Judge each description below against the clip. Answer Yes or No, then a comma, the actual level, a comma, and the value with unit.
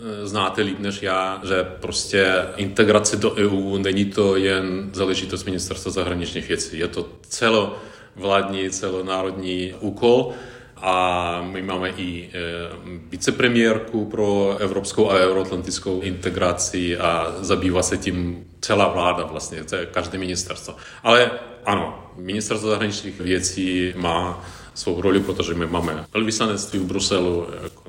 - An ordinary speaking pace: Yes, average, 125 wpm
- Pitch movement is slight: Yes, narrow, 2.0 semitones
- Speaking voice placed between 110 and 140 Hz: No, very low, 95 Hz